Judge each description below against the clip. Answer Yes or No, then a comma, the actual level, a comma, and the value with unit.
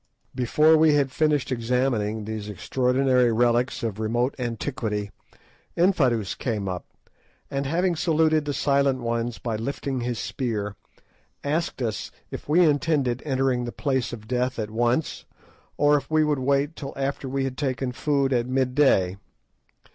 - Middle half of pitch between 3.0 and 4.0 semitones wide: Yes, average, 3.4 semitones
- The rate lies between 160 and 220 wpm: No, average, 150 wpm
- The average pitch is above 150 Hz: No, low, 130 Hz